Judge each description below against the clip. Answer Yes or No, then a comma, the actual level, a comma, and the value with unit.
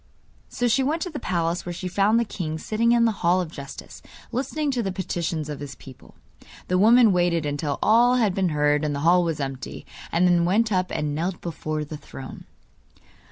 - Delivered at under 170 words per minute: No, fast, 205 wpm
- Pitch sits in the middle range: Yes, medium, 175 Hz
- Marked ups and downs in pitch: Yes, wide, 6.1 semitones